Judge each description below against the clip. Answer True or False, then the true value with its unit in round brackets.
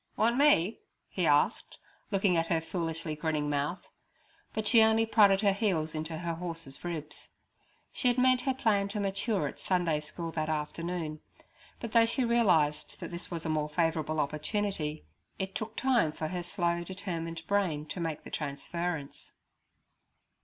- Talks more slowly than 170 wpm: True (160 wpm)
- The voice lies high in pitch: False (170 Hz)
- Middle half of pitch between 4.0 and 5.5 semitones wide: True (4.6 semitones)